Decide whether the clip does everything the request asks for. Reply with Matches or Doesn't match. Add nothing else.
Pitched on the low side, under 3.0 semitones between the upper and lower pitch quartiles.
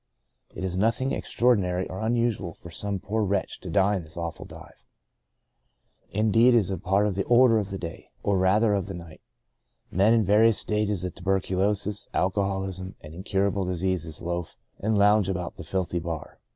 Matches